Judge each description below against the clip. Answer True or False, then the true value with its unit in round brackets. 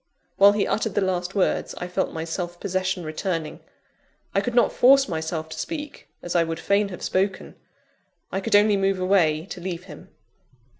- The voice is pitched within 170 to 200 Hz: True (185 Hz)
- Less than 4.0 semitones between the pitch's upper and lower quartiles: True (2.9 semitones)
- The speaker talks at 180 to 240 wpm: True (185 wpm)